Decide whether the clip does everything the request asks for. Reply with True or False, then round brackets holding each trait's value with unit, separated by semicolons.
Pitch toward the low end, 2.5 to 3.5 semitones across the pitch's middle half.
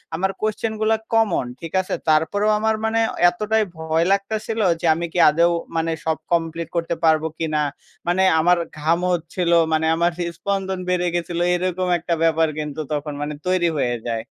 False (170 Hz; 3.1 semitones)